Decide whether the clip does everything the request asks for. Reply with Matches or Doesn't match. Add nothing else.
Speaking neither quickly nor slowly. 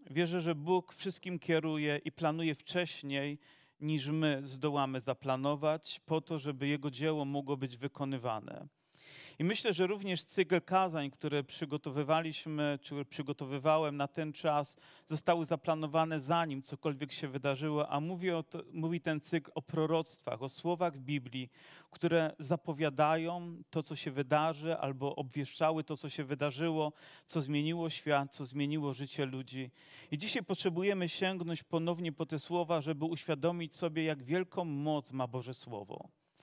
Matches